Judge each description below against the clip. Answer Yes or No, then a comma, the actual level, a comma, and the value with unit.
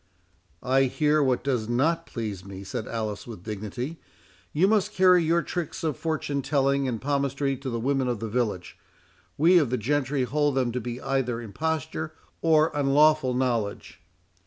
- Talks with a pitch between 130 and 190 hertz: Yes, low, 135 Hz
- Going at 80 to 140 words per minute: No, average, 160 wpm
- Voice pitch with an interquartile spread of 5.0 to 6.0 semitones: No, average, 4.3 semitones